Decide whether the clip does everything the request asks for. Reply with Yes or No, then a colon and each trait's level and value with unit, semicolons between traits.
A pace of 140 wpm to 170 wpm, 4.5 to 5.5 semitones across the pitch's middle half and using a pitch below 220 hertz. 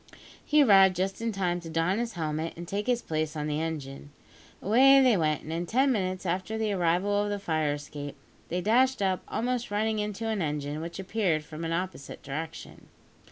No: average, 200 wpm; average, 5.1 semitones; medium, 185 Hz